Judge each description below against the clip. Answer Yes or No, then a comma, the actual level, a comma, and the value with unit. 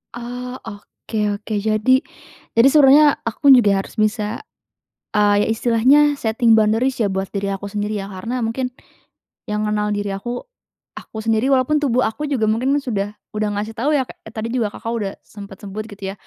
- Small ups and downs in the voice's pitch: No, average, 3.2 semitones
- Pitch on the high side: Yes, high, 220 Hz